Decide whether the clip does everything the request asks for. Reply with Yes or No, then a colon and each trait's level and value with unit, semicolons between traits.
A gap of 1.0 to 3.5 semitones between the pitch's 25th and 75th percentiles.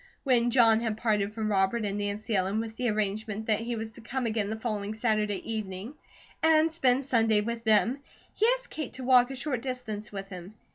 Yes: average, 2.8 semitones